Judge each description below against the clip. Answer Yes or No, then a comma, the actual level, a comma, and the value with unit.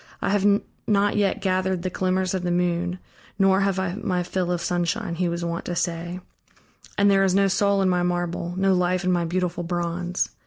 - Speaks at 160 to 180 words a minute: No, fast, 205 wpm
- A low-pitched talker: No, medium, 180 Hz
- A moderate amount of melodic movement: No, narrow, 1.7 semitones